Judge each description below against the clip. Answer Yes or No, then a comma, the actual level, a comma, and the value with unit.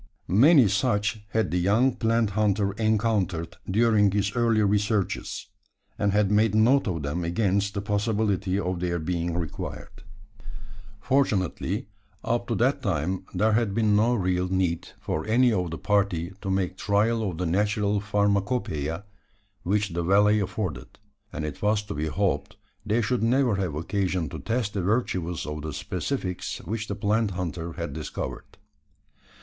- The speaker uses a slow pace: No, average, 155 wpm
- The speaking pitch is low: Yes, low, 100 Hz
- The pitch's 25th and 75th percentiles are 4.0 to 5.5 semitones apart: No, average, 3.2 semitones